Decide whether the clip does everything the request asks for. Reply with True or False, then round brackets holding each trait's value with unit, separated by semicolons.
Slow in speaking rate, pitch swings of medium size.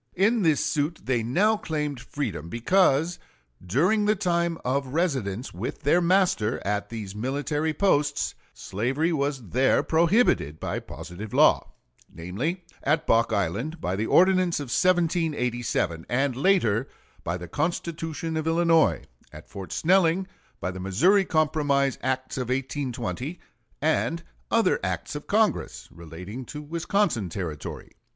False (130 wpm; 6.8 semitones)